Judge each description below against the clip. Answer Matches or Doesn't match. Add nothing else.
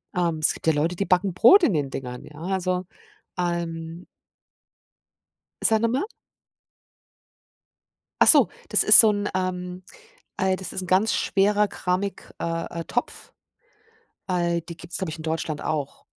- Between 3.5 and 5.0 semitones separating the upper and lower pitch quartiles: Doesn't match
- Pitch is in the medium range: Matches